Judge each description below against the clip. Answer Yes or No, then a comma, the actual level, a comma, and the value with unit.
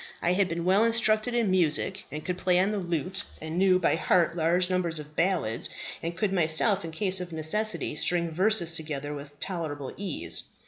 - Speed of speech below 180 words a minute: No, average, 190 wpm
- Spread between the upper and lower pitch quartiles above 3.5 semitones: No, average, 3.2 semitones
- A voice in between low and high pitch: Yes, medium, 175 Hz